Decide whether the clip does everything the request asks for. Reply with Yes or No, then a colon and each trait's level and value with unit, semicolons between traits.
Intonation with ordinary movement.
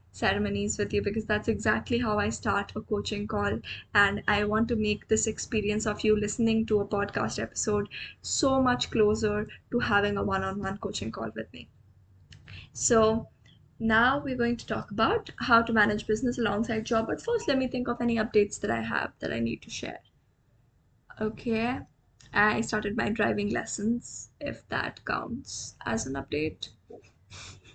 No: narrow, 1.9 semitones